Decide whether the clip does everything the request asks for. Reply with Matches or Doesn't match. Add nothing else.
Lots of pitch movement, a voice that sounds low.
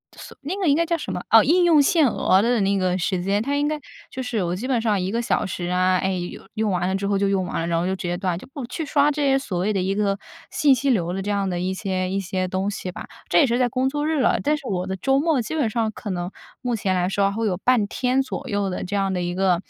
Doesn't match